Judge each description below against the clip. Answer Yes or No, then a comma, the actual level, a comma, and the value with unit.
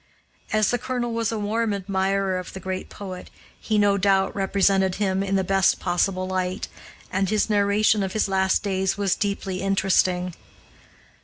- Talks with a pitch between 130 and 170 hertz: No, high, 195 Hz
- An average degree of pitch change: No, narrow, 1.5 semitones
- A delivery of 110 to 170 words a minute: Yes, average, 165 wpm